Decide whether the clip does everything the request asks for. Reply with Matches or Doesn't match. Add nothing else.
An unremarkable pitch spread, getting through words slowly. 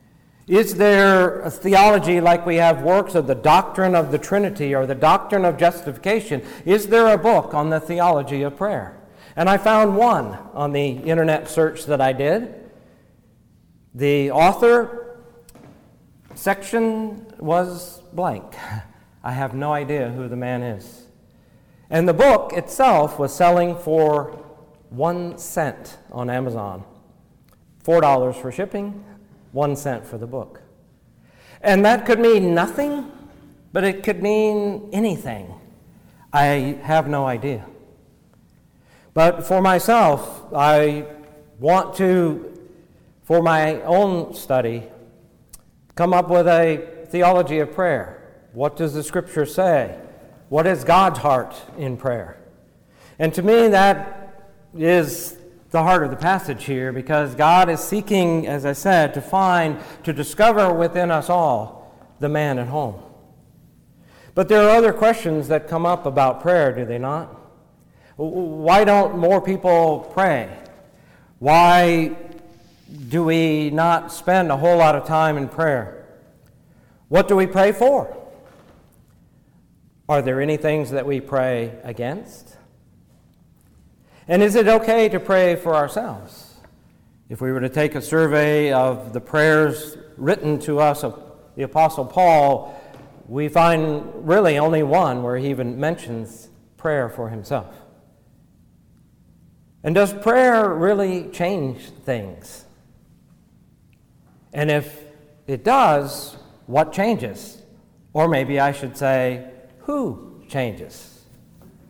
Matches